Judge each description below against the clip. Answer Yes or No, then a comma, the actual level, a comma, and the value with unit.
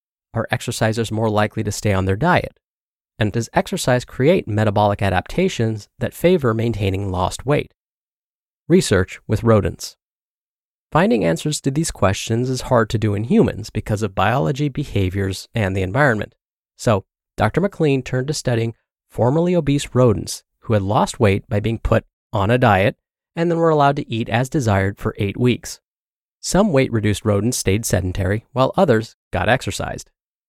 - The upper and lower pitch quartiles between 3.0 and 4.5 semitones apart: Yes, average, 4.2 semitones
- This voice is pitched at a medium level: No, low, 115 Hz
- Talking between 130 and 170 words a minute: Yes, average, 160 wpm